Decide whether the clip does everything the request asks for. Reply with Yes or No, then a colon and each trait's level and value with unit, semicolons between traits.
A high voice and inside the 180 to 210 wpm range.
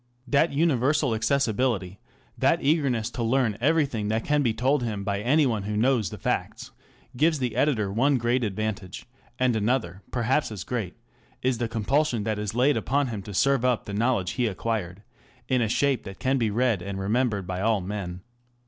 No: low, 115 Hz; average, 185 wpm